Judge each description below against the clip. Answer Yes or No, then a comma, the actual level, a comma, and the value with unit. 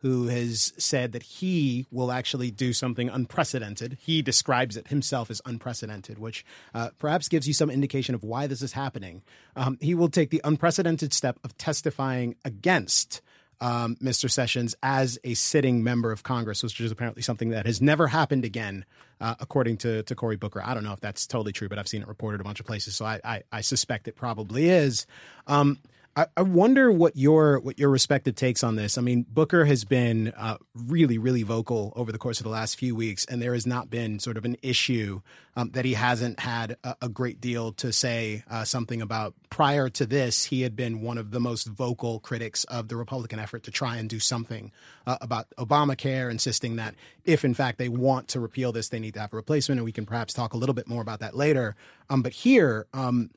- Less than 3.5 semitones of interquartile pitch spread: Yes, average, 2.8 semitones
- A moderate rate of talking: No, fast, 220 wpm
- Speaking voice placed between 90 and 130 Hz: Yes, low, 120 Hz